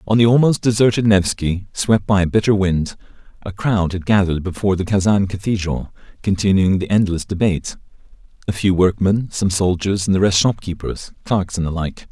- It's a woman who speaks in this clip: No, male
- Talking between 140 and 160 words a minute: No, average, 180 wpm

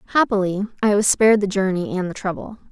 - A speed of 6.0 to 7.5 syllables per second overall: Yes, 6.5 syllables/s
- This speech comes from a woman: Yes, female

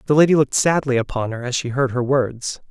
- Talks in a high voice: No, low, 130 Hz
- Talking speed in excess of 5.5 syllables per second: Yes, 6.0 syllables/s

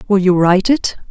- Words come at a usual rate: No, fast, 215 wpm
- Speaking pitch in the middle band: No, high, 195 Hz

